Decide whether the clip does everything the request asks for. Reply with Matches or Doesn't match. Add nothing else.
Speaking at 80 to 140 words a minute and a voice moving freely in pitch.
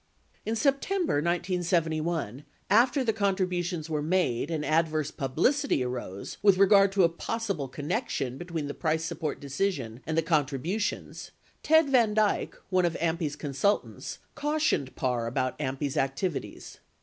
Matches